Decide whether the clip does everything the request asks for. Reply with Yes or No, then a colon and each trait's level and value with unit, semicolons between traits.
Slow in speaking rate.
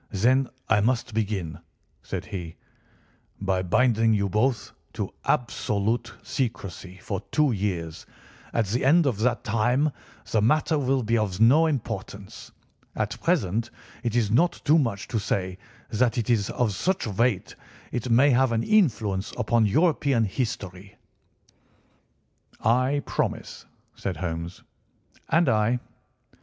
Yes: slow, 130 wpm